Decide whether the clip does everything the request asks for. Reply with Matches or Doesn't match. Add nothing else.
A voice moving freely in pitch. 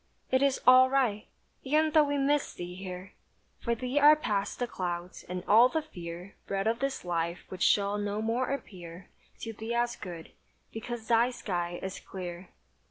Matches